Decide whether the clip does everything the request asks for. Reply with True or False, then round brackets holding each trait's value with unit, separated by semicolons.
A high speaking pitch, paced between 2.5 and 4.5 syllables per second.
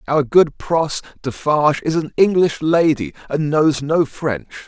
False (150 Hz; 4.1 syllables/s)